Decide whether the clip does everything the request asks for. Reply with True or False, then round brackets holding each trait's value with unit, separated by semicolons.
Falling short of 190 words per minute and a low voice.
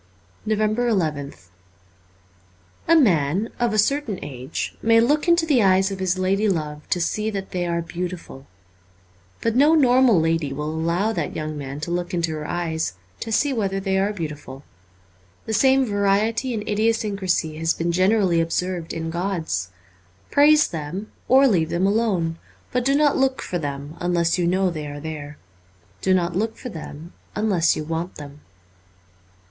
False (165 wpm; 185 Hz)